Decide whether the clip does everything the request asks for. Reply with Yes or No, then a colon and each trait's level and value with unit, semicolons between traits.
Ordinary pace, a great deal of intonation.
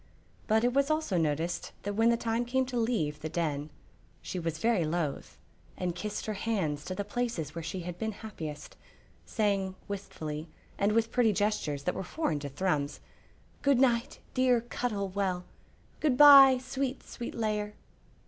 Yes: average, 165 wpm; wide, 6.1 semitones